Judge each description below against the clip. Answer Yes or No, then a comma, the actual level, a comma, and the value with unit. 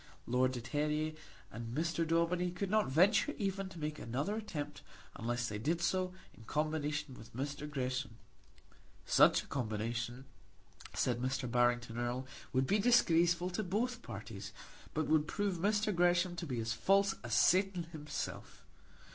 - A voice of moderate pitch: Yes, medium, 150 Hz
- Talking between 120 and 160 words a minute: Yes, average, 150 wpm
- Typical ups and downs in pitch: No, wide, 6.5 semitones